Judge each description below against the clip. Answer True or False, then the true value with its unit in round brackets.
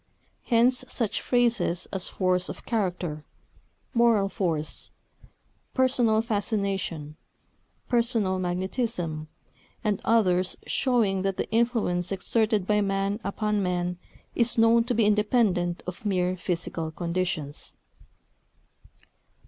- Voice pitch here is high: True (195 Hz)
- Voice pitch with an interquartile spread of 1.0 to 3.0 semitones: False (4.2 semitones)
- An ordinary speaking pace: False (100 wpm)